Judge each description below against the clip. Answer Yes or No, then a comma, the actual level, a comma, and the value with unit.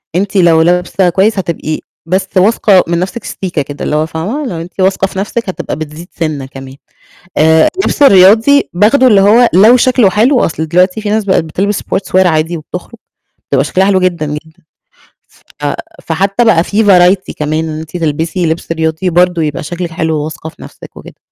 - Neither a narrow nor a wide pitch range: Yes, average, 3.8 semitones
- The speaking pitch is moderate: Yes, medium, 180 Hz